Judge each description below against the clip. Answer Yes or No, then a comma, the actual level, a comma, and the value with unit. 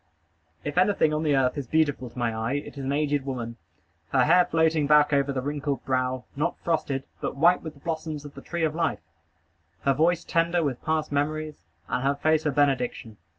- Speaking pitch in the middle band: Yes, medium, 145 Hz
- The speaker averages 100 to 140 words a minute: No, fast, 205 wpm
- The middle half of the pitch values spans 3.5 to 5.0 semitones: No, average, 2.8 semitones